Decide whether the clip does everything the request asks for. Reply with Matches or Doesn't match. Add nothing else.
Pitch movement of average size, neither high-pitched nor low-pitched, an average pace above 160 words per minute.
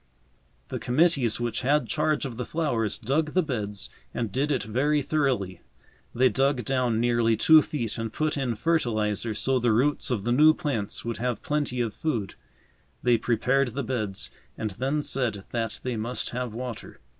Doesn't match